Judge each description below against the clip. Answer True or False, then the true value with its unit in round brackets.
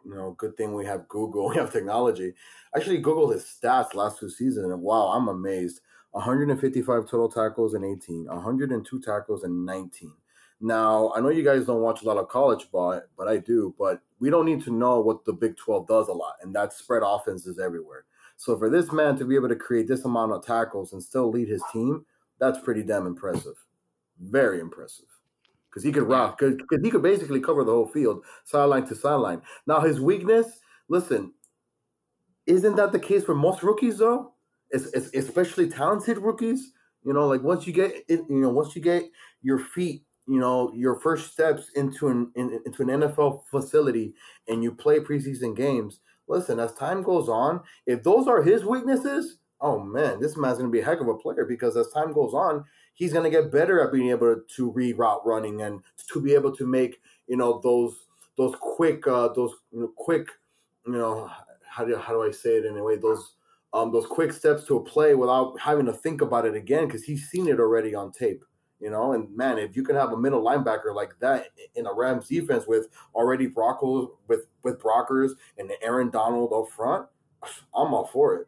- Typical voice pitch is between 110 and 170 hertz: True (135 Hz)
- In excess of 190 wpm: True (200 wpm)